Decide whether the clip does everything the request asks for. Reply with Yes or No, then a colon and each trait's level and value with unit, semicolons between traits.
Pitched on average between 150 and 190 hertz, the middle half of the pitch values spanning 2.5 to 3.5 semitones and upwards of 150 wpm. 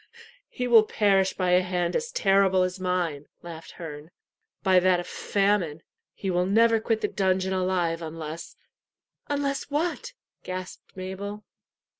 No: medium, 185 Hz; average, 2.8 semitones; average, 145 wpm